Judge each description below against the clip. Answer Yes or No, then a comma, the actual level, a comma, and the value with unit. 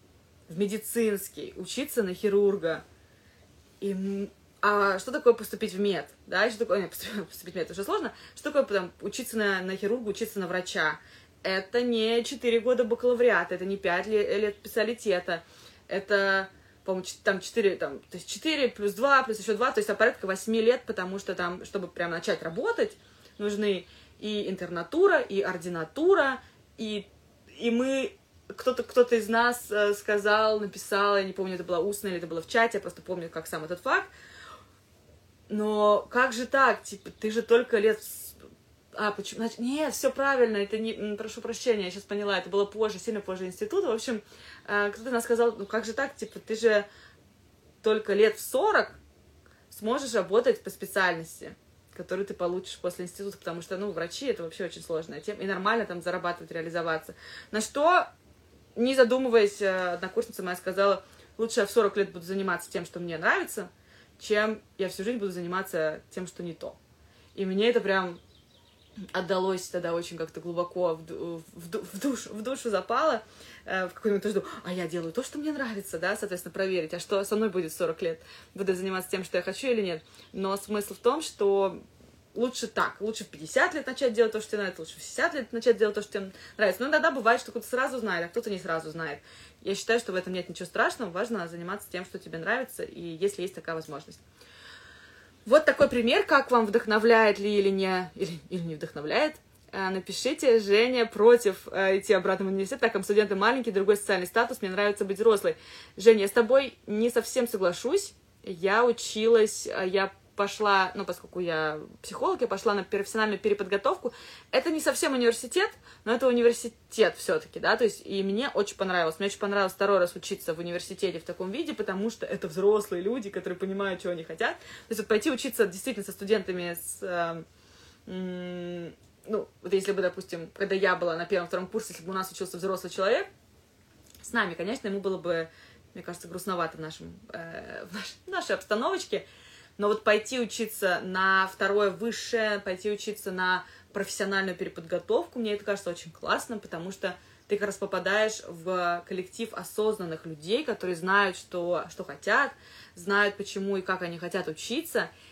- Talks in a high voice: Yes, high, 200 Hz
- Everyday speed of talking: No, fast, 185 wpm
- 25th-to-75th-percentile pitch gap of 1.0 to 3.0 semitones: No, average, 3.8 semitones